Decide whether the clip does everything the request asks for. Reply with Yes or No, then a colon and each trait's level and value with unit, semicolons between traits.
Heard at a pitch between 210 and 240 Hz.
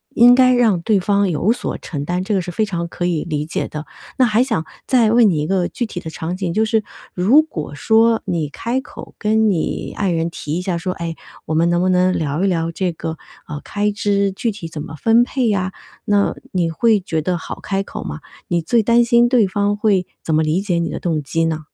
No: medium, 185 Hz